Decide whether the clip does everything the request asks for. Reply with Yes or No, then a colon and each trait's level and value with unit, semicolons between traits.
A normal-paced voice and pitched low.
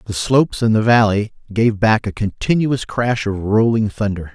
Yes: average, 180 wpm; low, 110 Hz